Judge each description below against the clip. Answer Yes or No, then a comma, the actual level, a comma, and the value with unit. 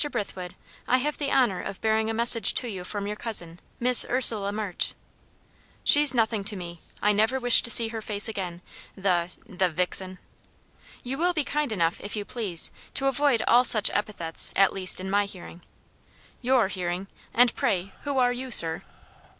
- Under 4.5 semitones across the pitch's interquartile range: No, average, 4.8 semitones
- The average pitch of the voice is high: Yes, high, 210 Hz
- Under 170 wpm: No, average, 180 wpm